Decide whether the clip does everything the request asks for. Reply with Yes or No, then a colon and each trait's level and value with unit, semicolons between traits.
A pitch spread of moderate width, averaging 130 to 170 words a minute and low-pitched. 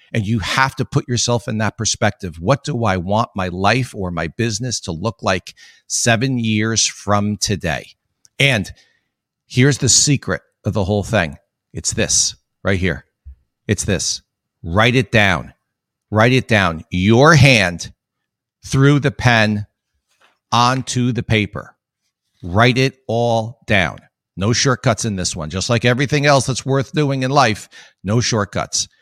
Yes: average, 4.5 semitones; average, 150 wpm; low, 110 Hz